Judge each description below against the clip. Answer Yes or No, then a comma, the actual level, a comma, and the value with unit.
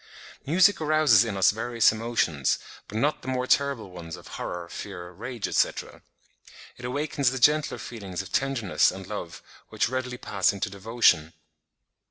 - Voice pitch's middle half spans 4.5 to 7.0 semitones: Yes, average, 5.3 semitones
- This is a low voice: Yes, low, 115 Hz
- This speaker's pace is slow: No, average, 155 wpm